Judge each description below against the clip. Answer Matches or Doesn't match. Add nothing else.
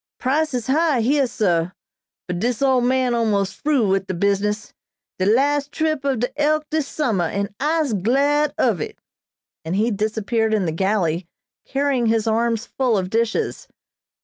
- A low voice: Doesn't match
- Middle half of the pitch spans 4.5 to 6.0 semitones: Matches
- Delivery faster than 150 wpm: Matches